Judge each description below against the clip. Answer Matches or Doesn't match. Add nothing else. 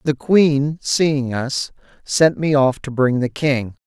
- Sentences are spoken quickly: Doesn't match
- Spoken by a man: Matches